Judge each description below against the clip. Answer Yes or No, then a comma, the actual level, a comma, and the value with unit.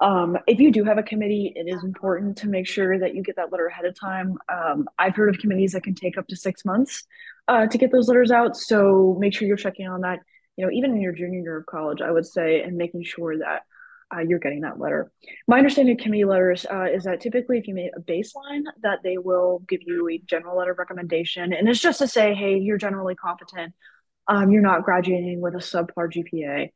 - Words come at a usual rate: No, fast, 240 wpm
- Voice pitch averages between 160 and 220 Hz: Yes, high, 190 Hz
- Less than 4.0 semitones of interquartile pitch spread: Yes, average, 3.4 semitones